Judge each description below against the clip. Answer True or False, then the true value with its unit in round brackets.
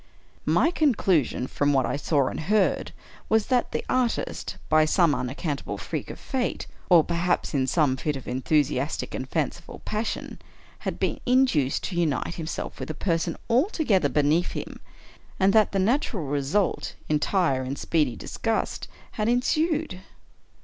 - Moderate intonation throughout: False (7.1 semitones)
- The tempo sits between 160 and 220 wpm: False (150 wpm)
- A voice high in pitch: False (170 Hz)